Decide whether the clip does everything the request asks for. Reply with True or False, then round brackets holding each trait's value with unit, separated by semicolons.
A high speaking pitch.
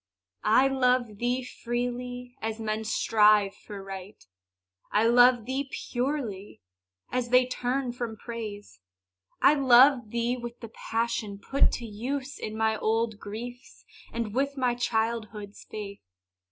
True (235 Hz)